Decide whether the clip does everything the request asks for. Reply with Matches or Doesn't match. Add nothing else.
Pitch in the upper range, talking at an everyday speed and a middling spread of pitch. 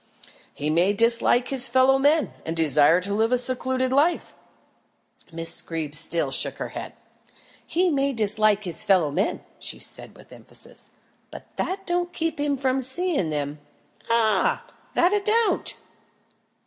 Doesn't match